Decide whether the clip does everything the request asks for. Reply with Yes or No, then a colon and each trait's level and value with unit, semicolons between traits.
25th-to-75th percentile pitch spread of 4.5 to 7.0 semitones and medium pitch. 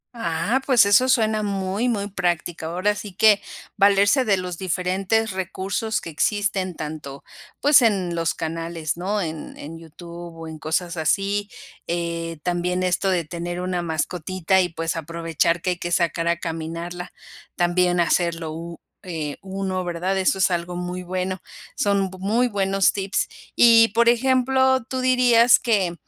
No: average, 3.2 semitones; medium, 180 Hz